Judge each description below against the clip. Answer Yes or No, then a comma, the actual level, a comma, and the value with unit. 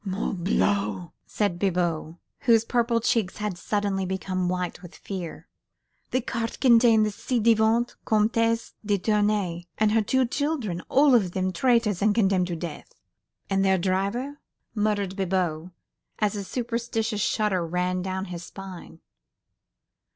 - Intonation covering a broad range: No, average, 3.8 semitones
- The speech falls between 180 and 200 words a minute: No, slow, 135 wpm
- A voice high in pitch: Yes, high, 205 Hz